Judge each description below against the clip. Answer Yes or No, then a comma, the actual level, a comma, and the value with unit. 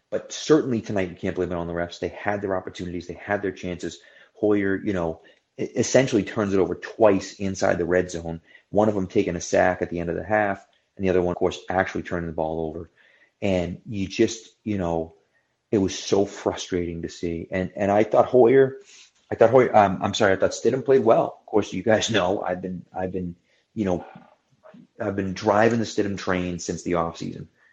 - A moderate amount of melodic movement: Yes, average, 3.1 semitones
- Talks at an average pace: No, fast, 215 wpm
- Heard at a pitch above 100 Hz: No, very low, 95 Hz